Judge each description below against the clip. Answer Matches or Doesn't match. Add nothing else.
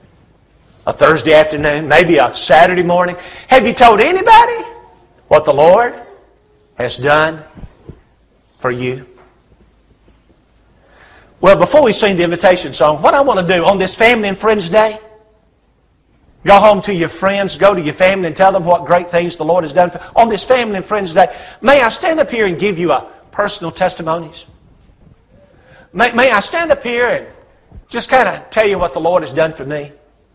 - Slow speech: Doesn't match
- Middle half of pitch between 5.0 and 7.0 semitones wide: Matches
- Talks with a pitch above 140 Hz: Matches